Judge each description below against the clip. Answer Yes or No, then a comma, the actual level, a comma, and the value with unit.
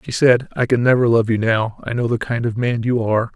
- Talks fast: Yes, fast, 285 wpm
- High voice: No, low, 115 Hz